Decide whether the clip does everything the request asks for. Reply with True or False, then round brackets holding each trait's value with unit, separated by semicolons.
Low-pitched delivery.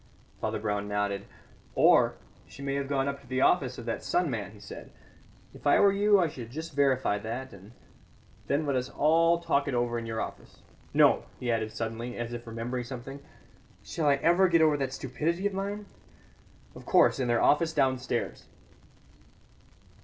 True (130 Hz)